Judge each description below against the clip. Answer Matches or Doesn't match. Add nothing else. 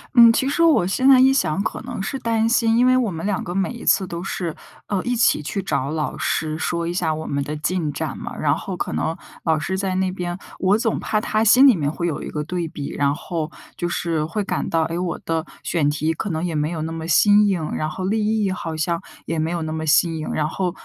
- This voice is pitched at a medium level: Matches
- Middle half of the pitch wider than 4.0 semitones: Matches